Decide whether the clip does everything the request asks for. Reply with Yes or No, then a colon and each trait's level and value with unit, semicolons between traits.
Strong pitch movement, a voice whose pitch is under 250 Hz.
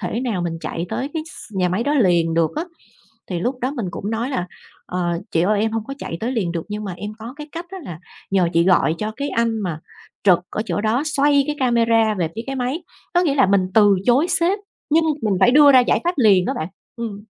Yes: wide, 6.8 semitones; high, 225 Hz